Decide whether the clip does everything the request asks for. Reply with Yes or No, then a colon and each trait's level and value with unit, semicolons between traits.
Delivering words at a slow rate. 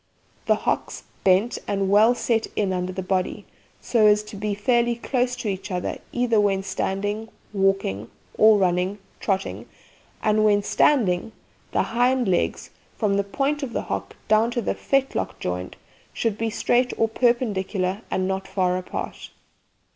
No: average, 155 wpm